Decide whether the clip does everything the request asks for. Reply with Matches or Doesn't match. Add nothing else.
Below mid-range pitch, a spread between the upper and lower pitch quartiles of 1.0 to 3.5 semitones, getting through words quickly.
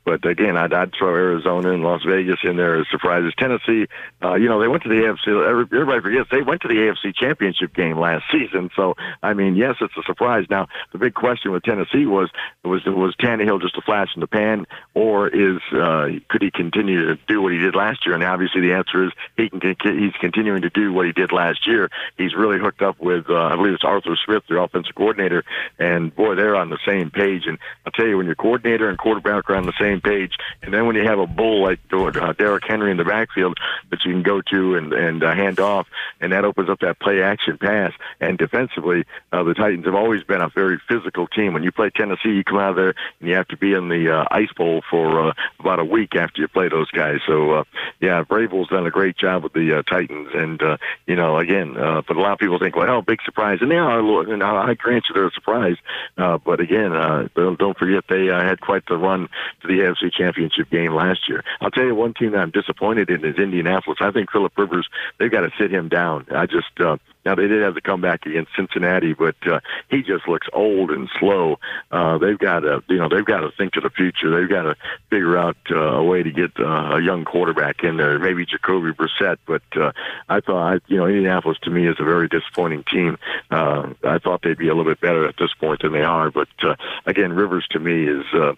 Matches